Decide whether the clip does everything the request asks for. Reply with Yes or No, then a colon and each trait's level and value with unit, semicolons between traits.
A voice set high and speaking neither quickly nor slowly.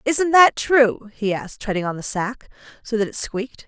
No: high, 230 Hz; fast, 210 wpm